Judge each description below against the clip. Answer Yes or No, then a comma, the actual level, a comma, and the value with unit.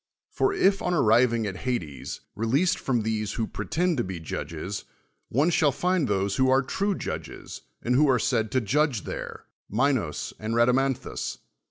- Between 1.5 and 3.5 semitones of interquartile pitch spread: No, average, 5.0 semitones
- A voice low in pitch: Yes, low, 125 Hz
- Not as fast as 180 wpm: Yes, average, 165 wpm